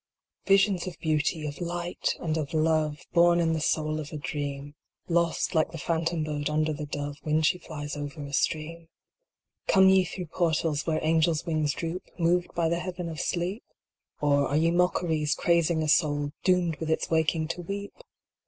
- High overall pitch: No, medium, 160 Hz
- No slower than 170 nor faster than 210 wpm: Yes, average, 180 wpm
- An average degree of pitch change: No, narrow, 2.1 semitones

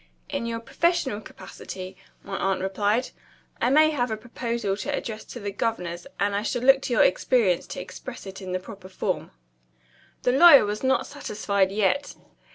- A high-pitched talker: Yes, high, 215 Hz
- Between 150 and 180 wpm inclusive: Yes, average, 175 wpm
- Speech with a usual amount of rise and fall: Yes, average, 4.4 semitones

